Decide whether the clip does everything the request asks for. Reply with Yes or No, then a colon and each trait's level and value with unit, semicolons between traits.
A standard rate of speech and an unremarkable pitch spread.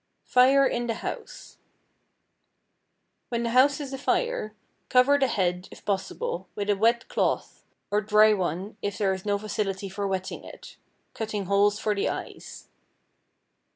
Yes: average, 150 wpm; average, 3.4 semitones